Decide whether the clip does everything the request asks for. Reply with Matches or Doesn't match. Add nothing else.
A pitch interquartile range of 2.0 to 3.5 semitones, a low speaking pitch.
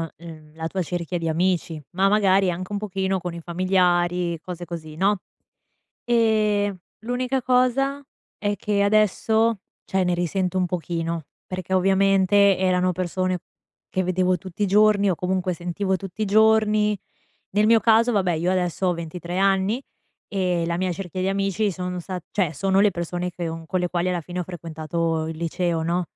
Doesn't match